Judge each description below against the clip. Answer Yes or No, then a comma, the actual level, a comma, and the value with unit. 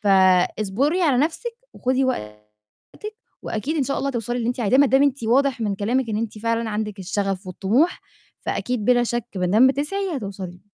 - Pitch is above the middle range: Yes, high, 230 Hz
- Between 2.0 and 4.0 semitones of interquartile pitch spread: No, average, 5.3 semitones